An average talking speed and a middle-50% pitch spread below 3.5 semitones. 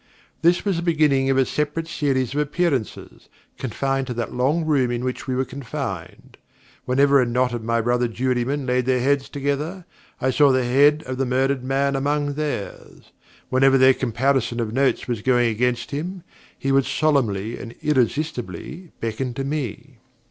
Yes: average, 170 wpm; average, 2.7 semitones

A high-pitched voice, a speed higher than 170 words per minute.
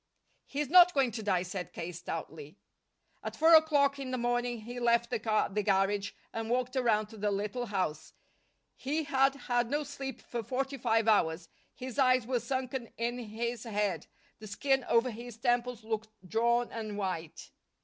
Yes: high, 235 Hz; average, 180 wpm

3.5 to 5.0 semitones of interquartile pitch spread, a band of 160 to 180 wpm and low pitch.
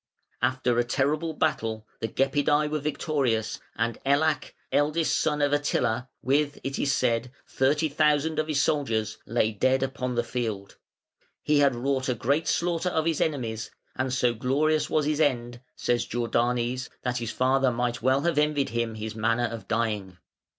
Yes: average, 3.9 semitones; average, 165 wpm; low, 130 Hz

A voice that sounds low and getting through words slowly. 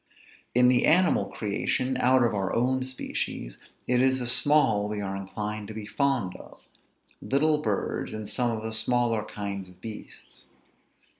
No: low, 115 Hz; average, 160 wpm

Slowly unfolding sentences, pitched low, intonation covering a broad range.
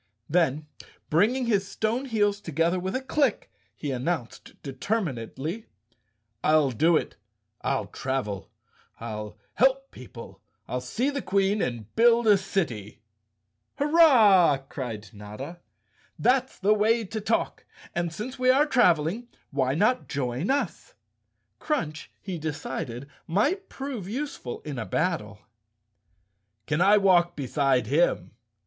No: slow, 125 wpm; medium, 175 Hz; wide, 8.9 semitones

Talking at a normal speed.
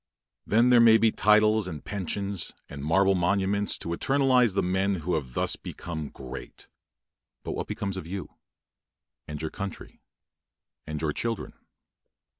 Yes: average, 145 wpm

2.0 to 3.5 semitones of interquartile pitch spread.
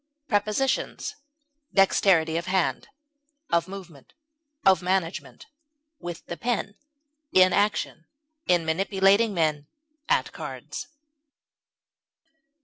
Yes: average, 3.0 semitones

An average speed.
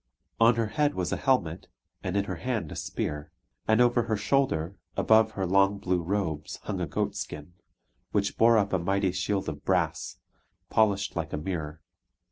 Yes: average, 180 wpm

